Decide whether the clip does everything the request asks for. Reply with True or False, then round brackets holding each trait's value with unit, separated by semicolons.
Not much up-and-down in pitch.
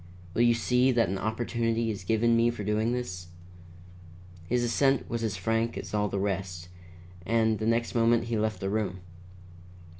True (2.2 semitones)